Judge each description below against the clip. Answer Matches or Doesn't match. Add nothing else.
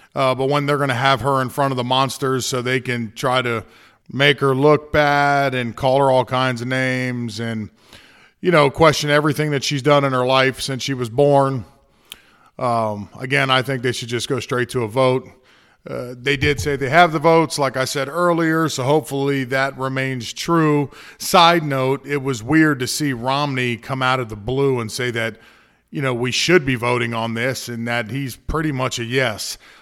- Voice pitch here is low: Matches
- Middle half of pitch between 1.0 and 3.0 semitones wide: Matches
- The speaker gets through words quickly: Matches